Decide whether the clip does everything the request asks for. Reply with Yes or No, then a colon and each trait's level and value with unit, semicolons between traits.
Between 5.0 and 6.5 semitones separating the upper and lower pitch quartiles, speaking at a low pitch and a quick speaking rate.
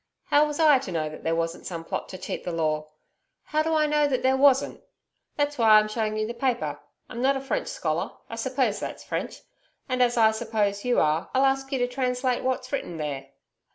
No: wide, 5.4 semitones; high, 245 Hz; fast, 225 wpm